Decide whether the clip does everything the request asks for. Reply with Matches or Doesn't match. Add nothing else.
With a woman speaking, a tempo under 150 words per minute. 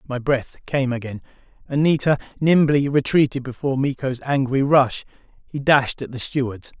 Doesn't match